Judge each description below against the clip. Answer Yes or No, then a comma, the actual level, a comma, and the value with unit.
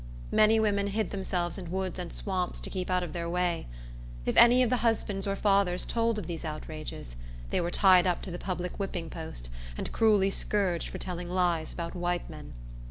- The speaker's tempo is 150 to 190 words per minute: No, average, 200 wpm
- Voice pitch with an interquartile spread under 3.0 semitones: Yes, narrow, 2.5 semitones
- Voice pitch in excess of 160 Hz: Yes, medium, 185 Hz